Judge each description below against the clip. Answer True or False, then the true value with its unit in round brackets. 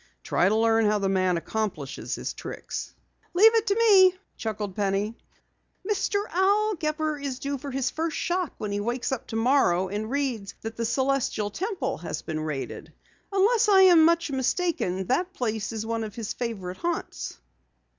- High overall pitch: True (250 Hz)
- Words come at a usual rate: True (170 wpm)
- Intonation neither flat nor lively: False (8.7 semitones)